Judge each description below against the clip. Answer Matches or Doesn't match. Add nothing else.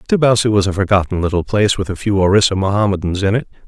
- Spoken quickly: Matches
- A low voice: Matches